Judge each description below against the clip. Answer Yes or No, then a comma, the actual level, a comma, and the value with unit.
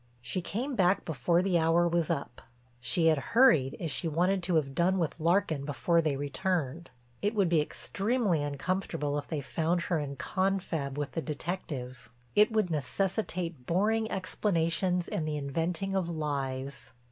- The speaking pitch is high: No, medium, 165 Hz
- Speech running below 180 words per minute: Yes, average, 160 wpm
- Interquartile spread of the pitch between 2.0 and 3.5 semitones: No, average, 4.2 semitones